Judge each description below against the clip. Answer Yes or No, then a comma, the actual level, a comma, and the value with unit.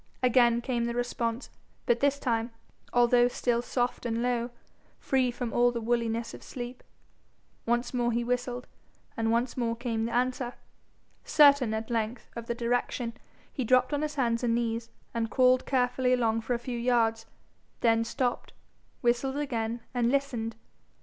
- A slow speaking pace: No, average, 160 wpm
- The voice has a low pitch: No, high, 240 Hz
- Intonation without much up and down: Yes, narrow, 1.4 semitones